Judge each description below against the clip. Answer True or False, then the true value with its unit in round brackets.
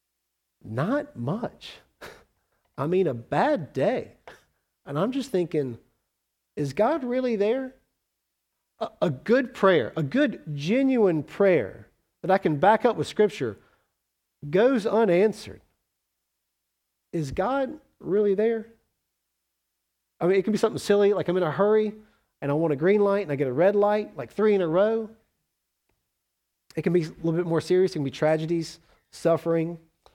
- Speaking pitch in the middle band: True (175 Hz)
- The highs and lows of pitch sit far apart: True (6.8 semitones)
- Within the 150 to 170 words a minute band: True (155 wpm)